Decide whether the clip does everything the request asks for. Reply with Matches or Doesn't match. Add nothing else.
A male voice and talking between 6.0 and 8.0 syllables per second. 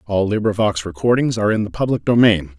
Matches